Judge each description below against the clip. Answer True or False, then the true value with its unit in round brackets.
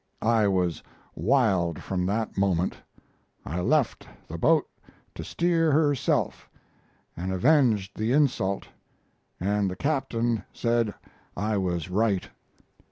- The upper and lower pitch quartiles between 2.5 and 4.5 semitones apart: False (5.2 semitones)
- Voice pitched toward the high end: False (105 Hz)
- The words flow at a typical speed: False (110 wpm)